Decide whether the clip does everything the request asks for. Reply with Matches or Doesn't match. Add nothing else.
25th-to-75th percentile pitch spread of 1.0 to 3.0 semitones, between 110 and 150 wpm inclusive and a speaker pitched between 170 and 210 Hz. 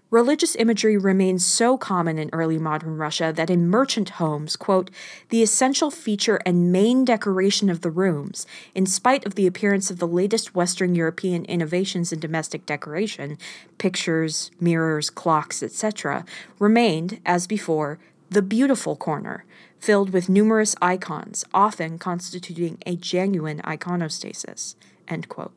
Doesn't match